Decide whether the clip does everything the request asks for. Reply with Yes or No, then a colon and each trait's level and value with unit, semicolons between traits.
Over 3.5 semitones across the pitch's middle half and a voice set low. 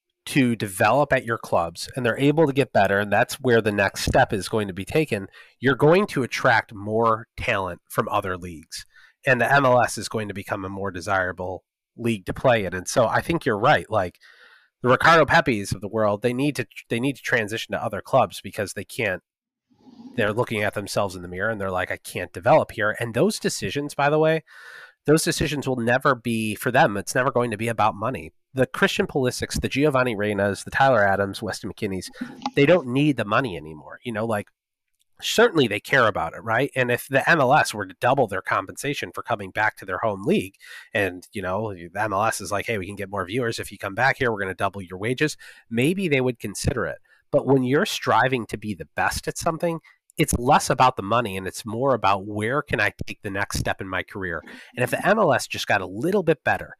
Yes: average, 5.3 semitones; low, 115 Hz